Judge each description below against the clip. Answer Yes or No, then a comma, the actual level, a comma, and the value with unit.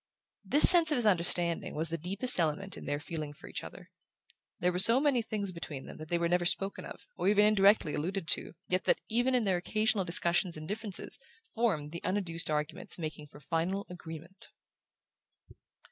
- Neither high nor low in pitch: Yes, medium, 180 Hz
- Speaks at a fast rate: No, average, 185 wpm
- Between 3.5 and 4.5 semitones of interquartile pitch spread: Yes, average, 4.1 semitones